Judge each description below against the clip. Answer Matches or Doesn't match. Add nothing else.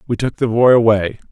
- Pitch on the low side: Matches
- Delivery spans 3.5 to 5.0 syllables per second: Doesn't match